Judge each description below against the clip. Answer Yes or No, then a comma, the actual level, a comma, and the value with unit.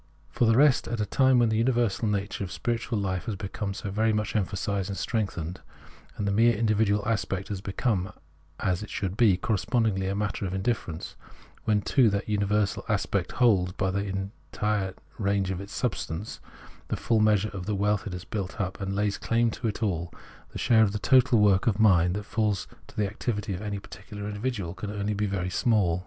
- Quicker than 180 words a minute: Yes, fast, 205 wpm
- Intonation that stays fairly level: Yes, narrow, 2.3 semitones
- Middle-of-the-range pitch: No, low, 105 Hz